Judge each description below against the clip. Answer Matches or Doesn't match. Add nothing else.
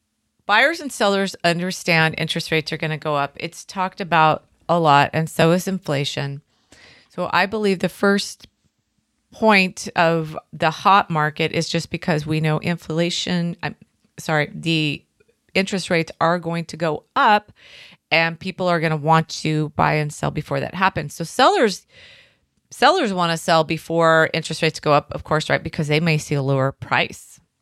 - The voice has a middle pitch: Matches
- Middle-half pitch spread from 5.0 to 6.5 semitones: Doesn't match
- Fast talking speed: Doesn't match